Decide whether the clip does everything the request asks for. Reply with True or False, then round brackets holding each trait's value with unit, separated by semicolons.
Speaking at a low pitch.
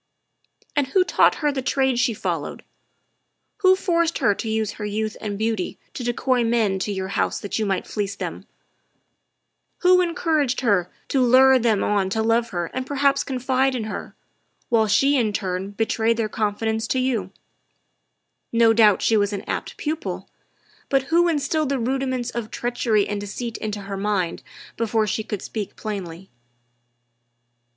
False (225 Hz)